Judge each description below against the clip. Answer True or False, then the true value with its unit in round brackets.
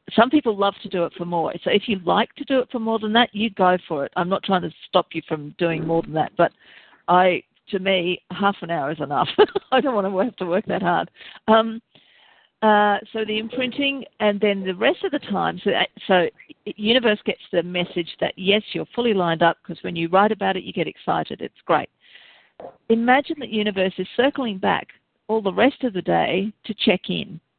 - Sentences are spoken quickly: True (220 wpm)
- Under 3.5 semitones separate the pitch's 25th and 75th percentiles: False (3.9 semitones)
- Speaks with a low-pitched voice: False (205 Hz)